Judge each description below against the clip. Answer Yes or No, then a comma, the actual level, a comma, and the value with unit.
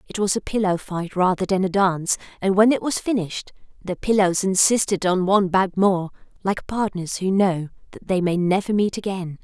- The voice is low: No, high, 190 Hz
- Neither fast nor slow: Yes, average, 195 wpm